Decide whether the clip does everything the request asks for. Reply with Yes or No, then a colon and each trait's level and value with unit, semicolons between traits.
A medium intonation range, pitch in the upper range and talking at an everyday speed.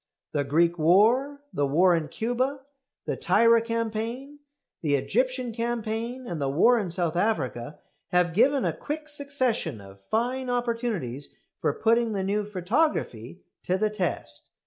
No: wide, 6.6 semitones; high, 220 Hz; average, 145 wpm